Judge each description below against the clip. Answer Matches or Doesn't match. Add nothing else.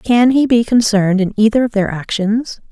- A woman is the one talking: Matches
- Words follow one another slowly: Doesn't match